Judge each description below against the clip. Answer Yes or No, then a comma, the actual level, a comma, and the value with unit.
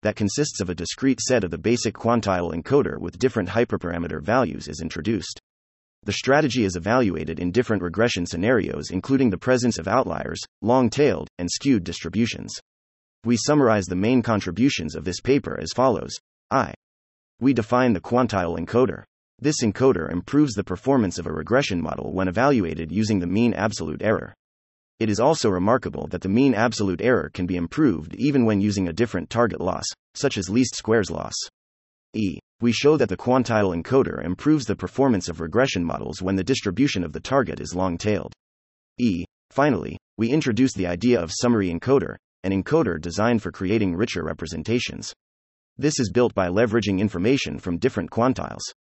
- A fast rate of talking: No, average, 170 wpm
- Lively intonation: Yes, wide, 6.1 semitones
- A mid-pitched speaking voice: No, low, 100 Hz